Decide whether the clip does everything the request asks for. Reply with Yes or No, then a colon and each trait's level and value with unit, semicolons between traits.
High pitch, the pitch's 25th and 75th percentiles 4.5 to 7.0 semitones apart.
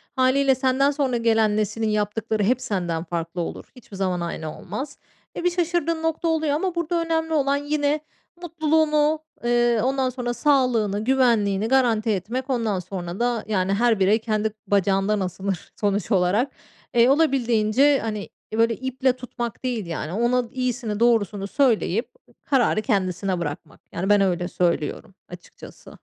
Yes: high, 230 Hz; average, 5.1 semitones